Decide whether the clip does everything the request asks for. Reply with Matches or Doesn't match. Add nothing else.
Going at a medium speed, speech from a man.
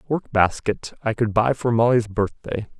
Matches